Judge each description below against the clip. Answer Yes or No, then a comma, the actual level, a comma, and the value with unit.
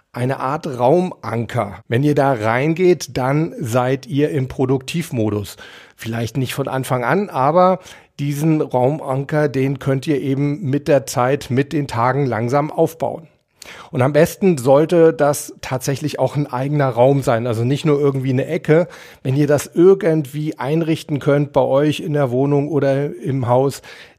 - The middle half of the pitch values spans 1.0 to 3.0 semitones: Yes, narrow, 2.6 semitones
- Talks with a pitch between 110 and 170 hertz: Yes, medium, 140 Hz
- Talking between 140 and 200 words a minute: Yes, average, 155 wpm